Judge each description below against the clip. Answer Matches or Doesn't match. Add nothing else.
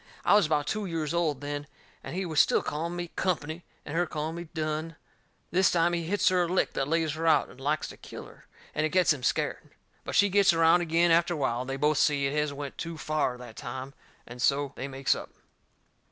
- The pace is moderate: Doesn't match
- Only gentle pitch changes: Doesn't match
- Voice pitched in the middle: Matches